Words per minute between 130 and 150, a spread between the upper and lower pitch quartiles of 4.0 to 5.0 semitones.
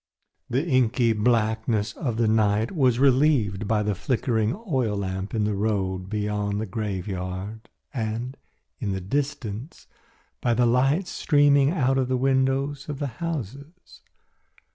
Yes: average, 140 wpm; average, 4.5 semitones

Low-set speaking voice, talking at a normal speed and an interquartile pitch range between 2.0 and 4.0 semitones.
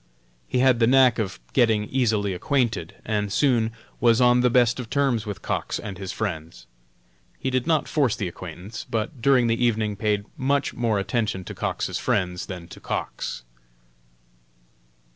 Yes: low, 115 Hz; average, 160 wpm; average, 3.7 semitones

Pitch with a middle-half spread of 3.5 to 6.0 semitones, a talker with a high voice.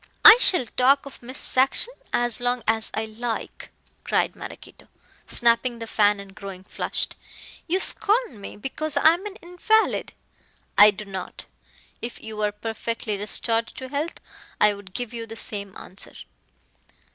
Yes: average, 4.4 semitones; high, 230 Hz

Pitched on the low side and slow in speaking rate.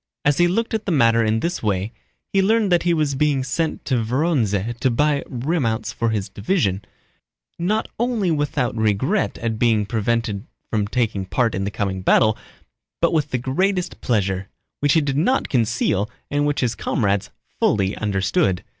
No: low, 120 Hz; average, 170 wpm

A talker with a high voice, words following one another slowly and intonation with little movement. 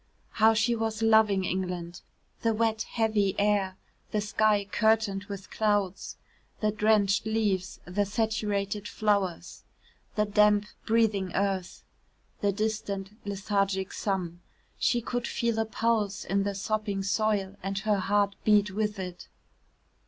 Yes: high, 205 Hz; slow, 130 wpm; narrow, 1.9 semitones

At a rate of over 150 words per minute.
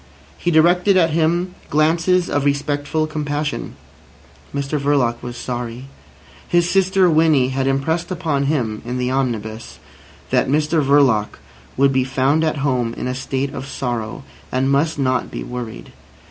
No: average, 145 wpm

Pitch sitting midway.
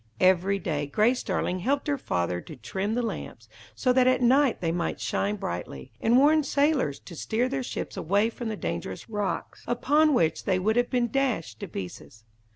No: high, 215 Hz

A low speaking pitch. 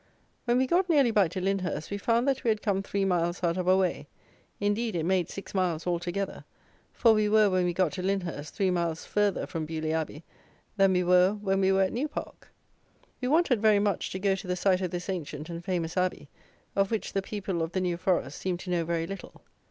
No: high, 190 Hz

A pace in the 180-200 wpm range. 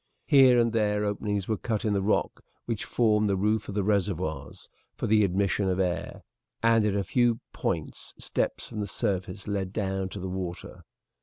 Yes: average, 185 wpm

